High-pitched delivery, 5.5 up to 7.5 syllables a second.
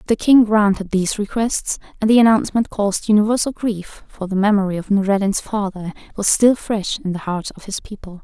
Yes: high, 205 Hz; 5.6 syllables/s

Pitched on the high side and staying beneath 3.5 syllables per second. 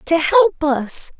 Yes: very high, 310 Hz; 2.9 syllables/s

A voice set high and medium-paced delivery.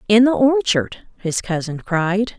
Yes: high, 210 Hz; average, 150 wpm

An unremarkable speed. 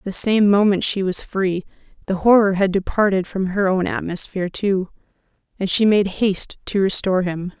Yes: average, 175 wpm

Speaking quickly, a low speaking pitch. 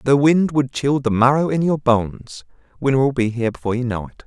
Yes: fast, 225 wpm; low, 130 Hz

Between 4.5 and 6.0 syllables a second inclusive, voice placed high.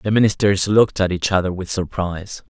No: 5.8 syllables/s; very low, 95 Hz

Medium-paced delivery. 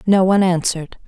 Yes: average, 165 wpm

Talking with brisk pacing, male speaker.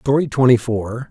No: average, 165 wpm; male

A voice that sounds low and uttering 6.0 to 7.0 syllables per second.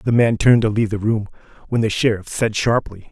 Yes: low, 110 Hz; 6.1 syllables/s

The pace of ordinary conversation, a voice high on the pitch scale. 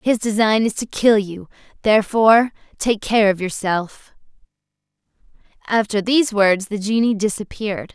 No: slow, 130 wpm; high, 210 Hz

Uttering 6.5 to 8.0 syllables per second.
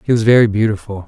Yes: 7.2 syllables/s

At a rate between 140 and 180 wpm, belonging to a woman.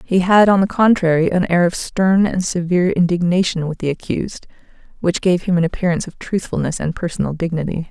No: average, 190 wpm; female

